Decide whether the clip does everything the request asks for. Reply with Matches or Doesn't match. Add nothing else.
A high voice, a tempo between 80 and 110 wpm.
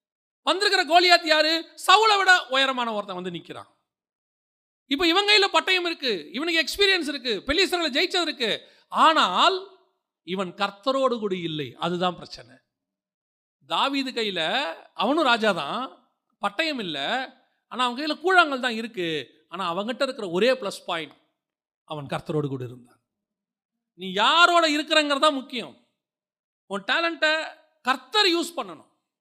Doesn't match